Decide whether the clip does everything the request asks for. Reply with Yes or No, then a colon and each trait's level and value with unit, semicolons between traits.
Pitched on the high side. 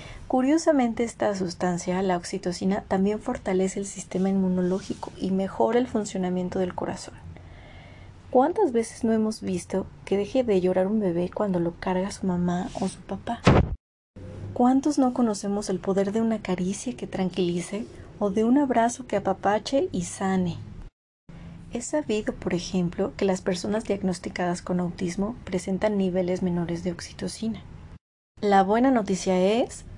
Yes: high, 195 Hz